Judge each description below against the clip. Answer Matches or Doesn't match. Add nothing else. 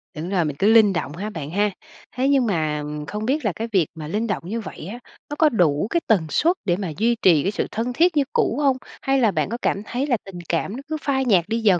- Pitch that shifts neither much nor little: Doesn't match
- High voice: Matches